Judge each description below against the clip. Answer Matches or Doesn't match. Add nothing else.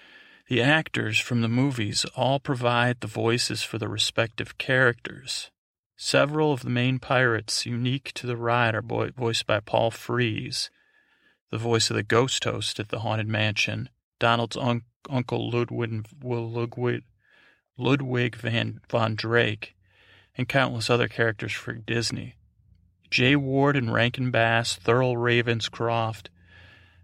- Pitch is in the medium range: Doesn't match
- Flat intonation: Matches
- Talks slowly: Matches